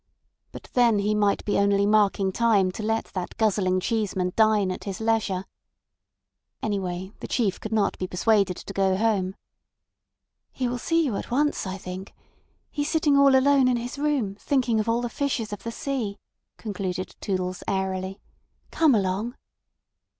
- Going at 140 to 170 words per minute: Yes, average, 165 wpm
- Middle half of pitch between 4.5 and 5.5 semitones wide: No, average, 4.0 semitones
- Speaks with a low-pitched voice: No, high, 210 Hz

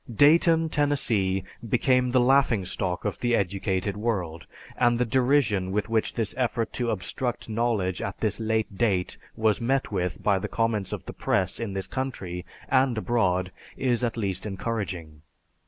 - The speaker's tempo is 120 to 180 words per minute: Yes, average, 155 wpm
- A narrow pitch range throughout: No, average, 4.4 semitones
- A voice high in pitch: No, low, 110 Hz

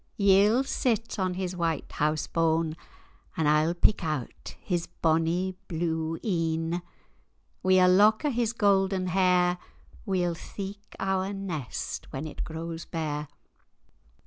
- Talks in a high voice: No, medium, 180 Hz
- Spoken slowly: Yes, slow, 125 wpm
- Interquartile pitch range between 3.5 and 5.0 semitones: No, average, 3.0 semitones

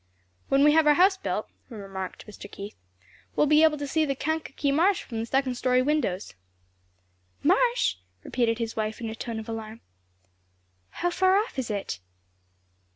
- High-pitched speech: Yes, very high, 270 Hz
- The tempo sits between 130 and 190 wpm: Yes, average, 165 wpm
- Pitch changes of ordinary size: No, wide, 6.0 semitones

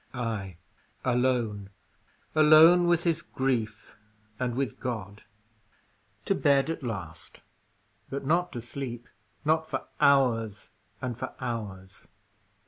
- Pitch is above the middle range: No, low, 125 Hz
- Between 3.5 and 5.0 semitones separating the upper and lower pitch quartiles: Yes, average, 4.4 semitones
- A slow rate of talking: Yes, slow, 110 wpm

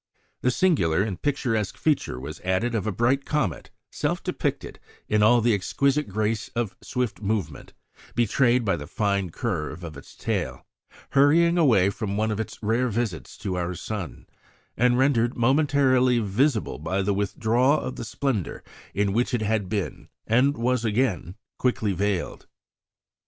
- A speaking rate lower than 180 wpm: Yes, average, 155 wpm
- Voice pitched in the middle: No, low, 110 Hz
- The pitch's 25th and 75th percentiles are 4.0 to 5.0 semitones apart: Yes, average, 4.3 semitones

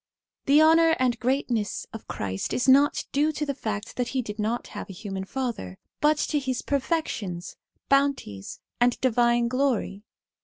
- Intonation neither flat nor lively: Yes, average, 4.9 semitones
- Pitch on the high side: Yes, very high, 250 Hz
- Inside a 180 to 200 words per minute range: No, average, 160 wpm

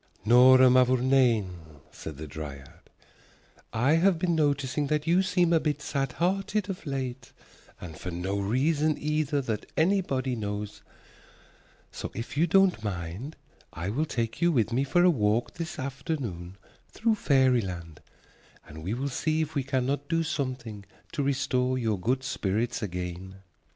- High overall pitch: No, low, 130 Hz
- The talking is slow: No, average, 150 wpm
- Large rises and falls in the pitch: Yes, wide, 6.7 semitones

